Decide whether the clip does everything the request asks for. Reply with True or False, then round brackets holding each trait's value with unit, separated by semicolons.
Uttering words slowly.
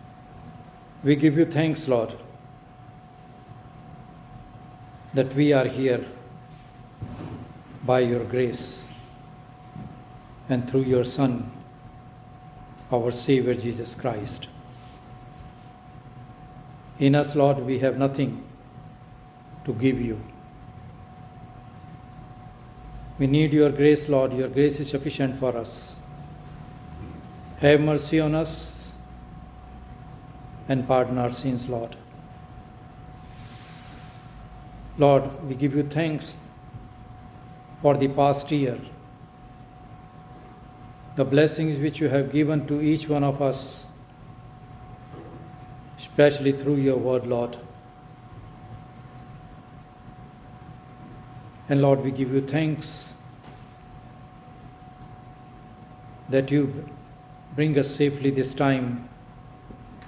True (85 wpm)